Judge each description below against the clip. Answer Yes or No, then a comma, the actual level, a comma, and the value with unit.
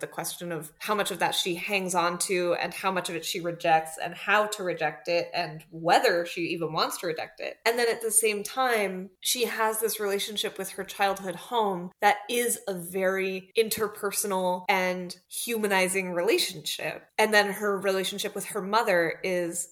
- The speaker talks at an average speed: Yes, average, 185 wpm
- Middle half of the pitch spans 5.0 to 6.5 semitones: No, average, 3.0 semitones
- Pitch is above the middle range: Yes, high, 195 Hz